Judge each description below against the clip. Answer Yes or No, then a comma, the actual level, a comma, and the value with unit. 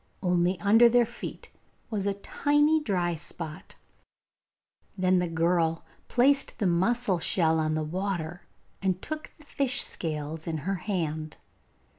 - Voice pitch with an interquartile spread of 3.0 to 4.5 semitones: No, average, 5.3 semitones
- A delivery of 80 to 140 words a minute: Yes, slow, 135 wpm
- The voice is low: No, medium, 180 Hz